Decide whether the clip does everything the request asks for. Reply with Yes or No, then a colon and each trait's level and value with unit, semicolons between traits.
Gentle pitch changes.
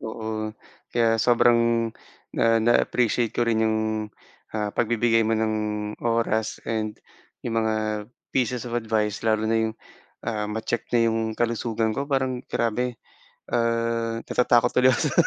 Yes: narrow, 1.2 semitones